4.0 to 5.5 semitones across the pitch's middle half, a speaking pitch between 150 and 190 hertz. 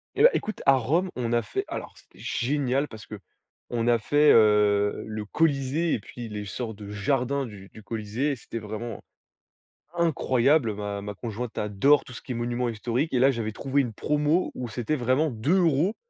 No: average, 4.6 semitones; low, 120 Hz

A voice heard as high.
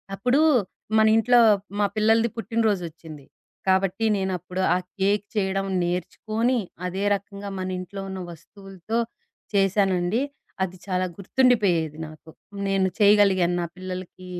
Yes: high, 195 Hz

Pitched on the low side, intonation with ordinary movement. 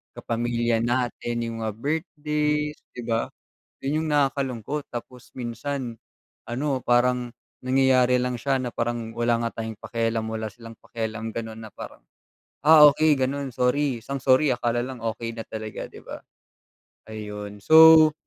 Yes: low, 120 Hz; average, 3.3 semitones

